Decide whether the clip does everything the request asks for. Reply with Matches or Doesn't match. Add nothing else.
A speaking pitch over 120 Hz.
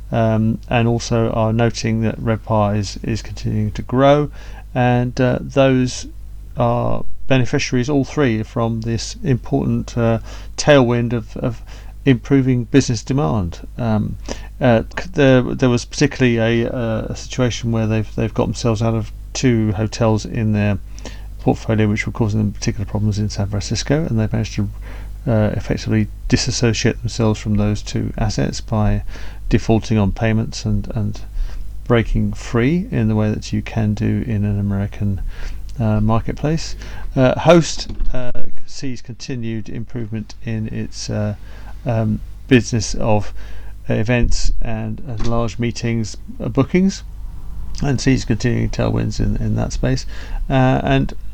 Doesn't match